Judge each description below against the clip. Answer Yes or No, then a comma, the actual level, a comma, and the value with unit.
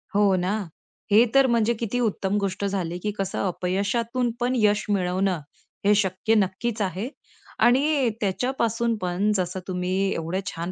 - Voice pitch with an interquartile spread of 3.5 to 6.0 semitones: Yes, average, 3.8 semitones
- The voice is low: No, high, 200 Hz